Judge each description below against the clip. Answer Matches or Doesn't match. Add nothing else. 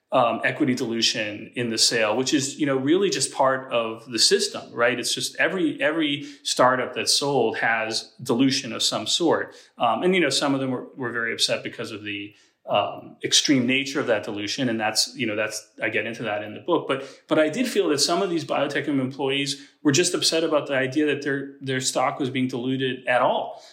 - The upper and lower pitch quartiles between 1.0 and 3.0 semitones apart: Doesn't match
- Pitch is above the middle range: Doesn't match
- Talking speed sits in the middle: Doesn't match